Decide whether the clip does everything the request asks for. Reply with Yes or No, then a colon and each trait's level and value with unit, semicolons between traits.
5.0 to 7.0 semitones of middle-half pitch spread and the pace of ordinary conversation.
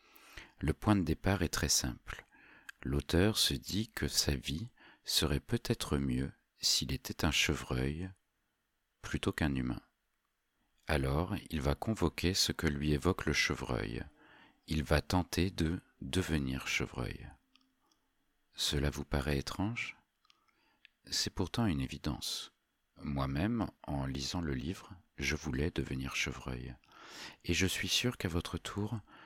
No: wide, 5.6 semitones; slow, 130 wpm